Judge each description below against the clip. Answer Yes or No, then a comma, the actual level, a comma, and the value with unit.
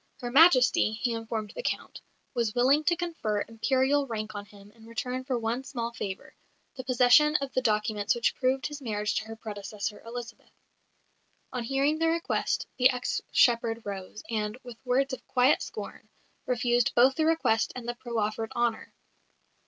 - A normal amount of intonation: Yes, average, 3.1 semitones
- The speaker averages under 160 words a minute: No, average, 170 wpm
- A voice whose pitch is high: Yes, high, 240 Hz